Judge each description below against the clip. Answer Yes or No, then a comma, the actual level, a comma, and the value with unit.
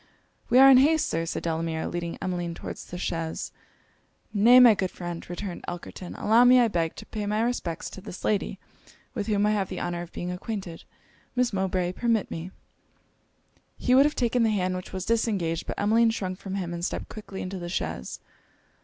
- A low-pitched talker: No, high, 190 Hz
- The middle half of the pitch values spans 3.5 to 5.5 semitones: Yes, average, 4.4 semitones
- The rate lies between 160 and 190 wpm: No, average, 200 wpm